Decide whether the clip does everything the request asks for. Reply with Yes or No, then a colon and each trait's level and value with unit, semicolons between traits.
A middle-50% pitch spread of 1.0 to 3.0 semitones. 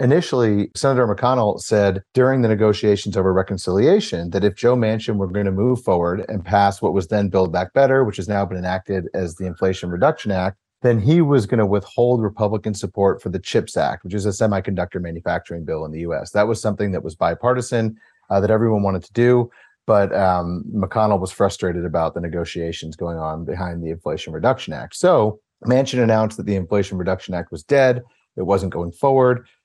No: average, 3.4 semitones